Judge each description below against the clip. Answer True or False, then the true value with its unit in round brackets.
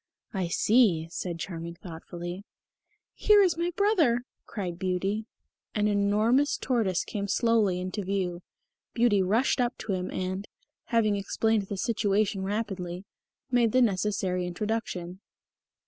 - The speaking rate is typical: False (125 wpm)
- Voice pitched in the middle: False (200 Hz)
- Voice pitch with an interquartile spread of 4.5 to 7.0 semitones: False (3.8 semitones)